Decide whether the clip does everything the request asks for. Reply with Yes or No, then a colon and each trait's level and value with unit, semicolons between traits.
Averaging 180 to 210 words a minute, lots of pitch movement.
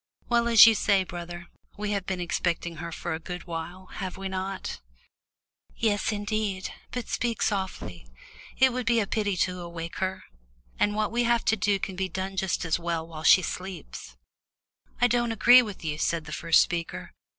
No: average, 185 wpm; average, 3.9 semitones